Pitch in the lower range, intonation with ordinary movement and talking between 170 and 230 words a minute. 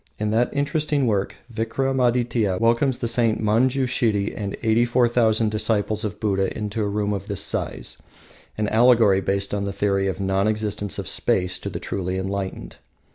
Yes: low, 110 Hz; average, 3.0 semitones; average, 175 wpm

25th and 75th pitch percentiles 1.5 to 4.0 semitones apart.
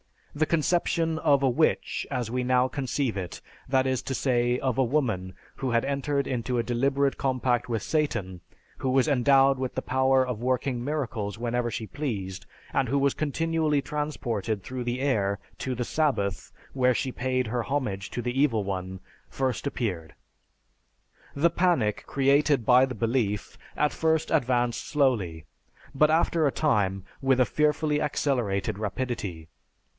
Yes: average, 3.5 semitones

